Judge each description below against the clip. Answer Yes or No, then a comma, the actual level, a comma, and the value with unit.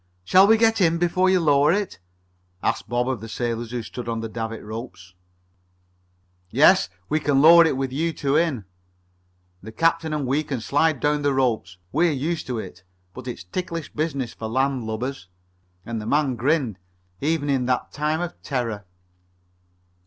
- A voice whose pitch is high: No, low, 135 Hz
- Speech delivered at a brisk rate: No, average, 175 wpm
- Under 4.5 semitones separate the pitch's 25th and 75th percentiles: No, wide, 5.4 semitones